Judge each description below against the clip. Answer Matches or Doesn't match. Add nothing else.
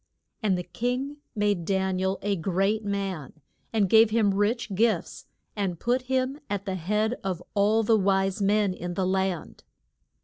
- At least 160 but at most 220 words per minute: Matches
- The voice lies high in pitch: Matches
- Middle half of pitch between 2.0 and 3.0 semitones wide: Matches